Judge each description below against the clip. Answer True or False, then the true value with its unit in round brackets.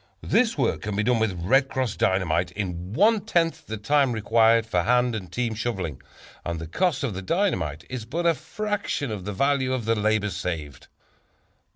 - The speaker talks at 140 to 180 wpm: False (190 wpm)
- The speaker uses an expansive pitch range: True (6.5 semitones)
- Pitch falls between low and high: False (110 Hz)